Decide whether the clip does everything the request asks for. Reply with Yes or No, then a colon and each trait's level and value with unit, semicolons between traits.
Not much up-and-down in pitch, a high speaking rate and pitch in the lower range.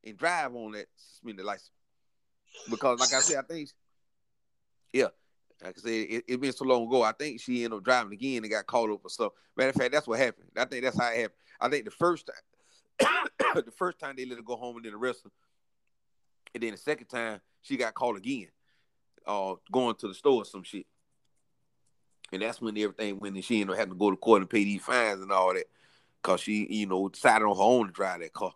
No: average, 4.1 semitones; fast, 245 wpm; low, 120 Hz